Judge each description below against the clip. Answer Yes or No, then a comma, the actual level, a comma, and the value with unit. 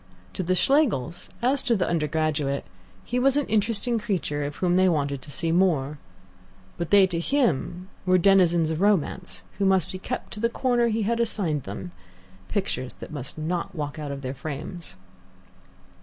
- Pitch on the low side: No, medium, 180 Hz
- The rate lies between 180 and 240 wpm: No, average, 170 wpm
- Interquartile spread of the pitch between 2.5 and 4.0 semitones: No, wide, 5.6 semitones